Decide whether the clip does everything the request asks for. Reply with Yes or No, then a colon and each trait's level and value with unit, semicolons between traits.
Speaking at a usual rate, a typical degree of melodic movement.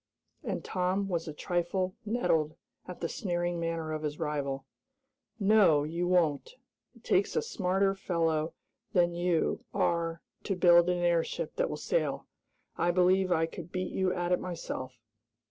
No: average, 155 wpm; narrow, 2.1 semitones